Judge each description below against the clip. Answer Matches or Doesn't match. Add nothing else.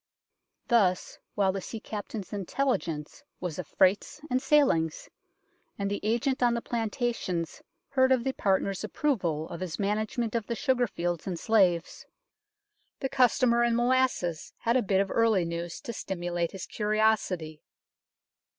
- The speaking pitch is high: Matches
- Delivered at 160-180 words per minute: Doesn't match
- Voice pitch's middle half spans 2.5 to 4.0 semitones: Doesn't match